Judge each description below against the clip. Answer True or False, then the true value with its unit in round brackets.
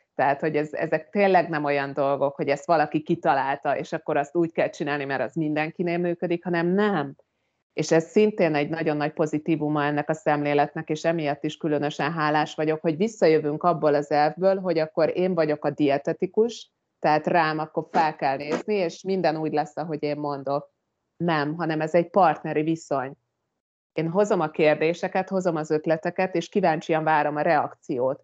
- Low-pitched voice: False (155 Hz)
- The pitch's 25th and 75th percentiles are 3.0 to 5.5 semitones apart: False (2.5 semitones)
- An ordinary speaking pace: False (175 wpm)